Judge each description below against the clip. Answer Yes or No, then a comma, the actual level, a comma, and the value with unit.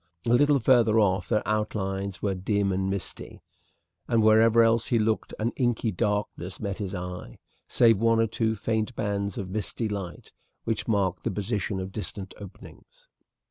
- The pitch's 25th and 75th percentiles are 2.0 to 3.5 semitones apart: Yes, narrow, 2.6 semitones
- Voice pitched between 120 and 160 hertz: No, low, 105 Hz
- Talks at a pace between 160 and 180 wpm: Yes, average, 165 wpm